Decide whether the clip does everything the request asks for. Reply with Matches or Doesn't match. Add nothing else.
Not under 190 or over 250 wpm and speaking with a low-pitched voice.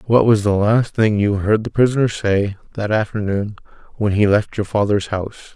Matches